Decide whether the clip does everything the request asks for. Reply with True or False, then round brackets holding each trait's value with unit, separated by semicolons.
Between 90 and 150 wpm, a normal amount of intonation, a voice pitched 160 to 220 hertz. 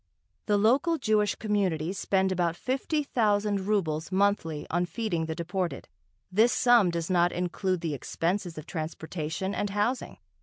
True (145 wpm; 3.7 semitones; 190 Hz)